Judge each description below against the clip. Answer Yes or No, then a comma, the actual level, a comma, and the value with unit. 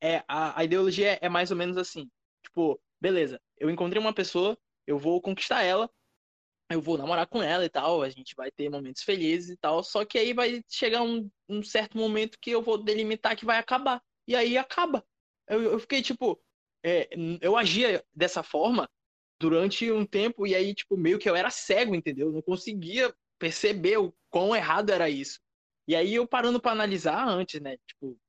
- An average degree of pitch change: No, wide, 5.7 semitones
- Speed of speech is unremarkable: No, fast, 195 wpm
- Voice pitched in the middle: No, high, 200 Hz